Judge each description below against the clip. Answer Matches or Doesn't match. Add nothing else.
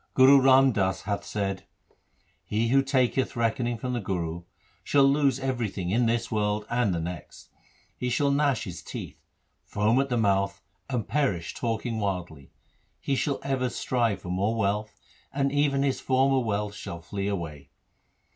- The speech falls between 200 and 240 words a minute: Doesn't match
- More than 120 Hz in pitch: Doesn't match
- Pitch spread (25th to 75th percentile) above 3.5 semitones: Matches